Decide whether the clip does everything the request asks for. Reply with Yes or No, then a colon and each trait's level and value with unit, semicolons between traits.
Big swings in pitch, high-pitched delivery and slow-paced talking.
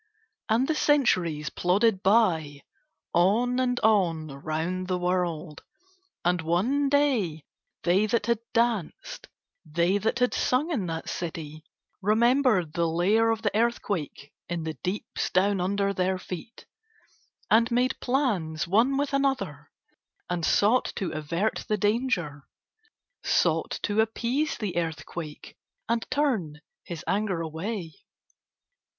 Yes: wide, 5.9 semitones; high, 195 Hz; slow, 125 wpm